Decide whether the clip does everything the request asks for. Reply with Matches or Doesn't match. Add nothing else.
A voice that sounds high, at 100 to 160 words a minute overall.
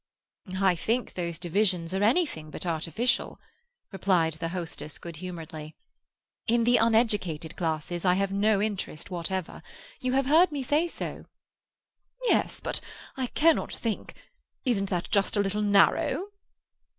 Matches